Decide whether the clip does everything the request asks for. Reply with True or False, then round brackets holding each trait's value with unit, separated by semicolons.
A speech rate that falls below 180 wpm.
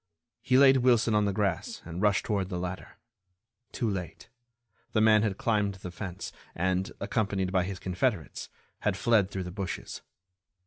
True (160 wpm)